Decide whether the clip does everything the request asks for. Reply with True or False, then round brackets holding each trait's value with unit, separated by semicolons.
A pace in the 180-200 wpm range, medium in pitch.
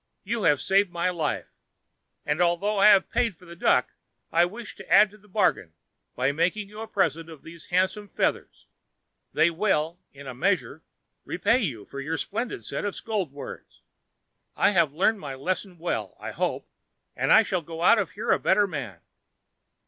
True (185 wpm; 180 Hz)